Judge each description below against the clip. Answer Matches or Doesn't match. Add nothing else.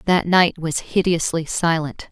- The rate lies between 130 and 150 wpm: Matches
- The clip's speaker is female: Matches